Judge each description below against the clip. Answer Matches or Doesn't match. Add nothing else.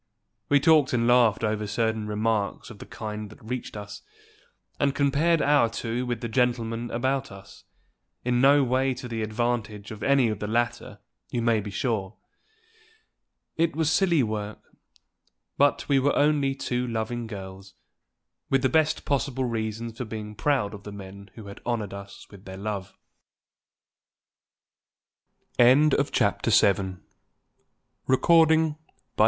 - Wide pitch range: Doesn't match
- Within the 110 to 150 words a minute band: Matches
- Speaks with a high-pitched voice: Doesn't match